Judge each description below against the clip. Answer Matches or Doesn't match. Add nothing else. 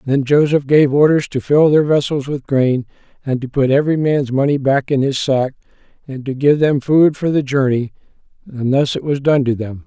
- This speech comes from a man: Matches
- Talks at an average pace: Doesn't match